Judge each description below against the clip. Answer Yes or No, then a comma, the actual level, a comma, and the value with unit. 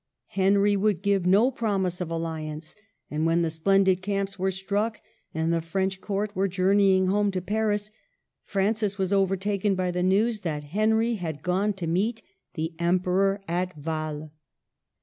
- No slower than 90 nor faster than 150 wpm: No, average, 160 wpm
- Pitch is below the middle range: No, high, 190 Hz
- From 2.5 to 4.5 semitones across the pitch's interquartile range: Yes, average, 2.9 semitones